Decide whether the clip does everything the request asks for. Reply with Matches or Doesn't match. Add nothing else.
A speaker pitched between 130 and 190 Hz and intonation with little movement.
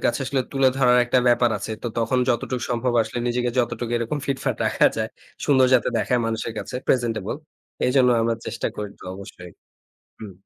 Doesn't match